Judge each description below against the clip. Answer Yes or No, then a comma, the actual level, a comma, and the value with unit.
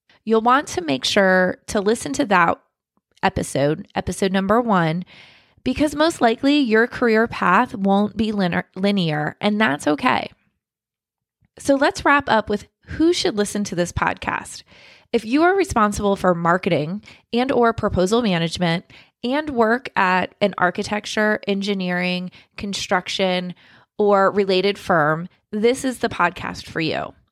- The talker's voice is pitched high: Yes, high, 205 Hz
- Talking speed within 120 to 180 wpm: Yes, average, 140 wpm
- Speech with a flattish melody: No, average, 4.5 semitones